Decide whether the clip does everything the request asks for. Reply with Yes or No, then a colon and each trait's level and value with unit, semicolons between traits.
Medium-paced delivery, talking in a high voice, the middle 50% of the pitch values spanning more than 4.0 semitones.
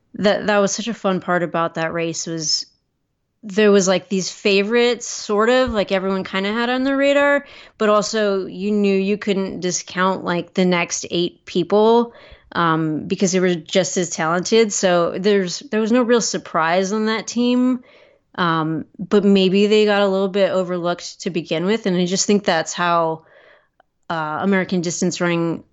No: average, 180 wpm; high, 195 Hz; average, 3.4 semitones